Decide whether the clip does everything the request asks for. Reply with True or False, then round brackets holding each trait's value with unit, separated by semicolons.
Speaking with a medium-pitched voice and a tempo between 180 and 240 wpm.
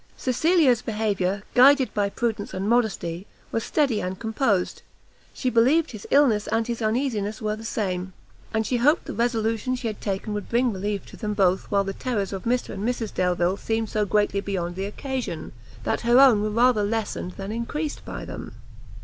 False (220 Hz; 185 wpm)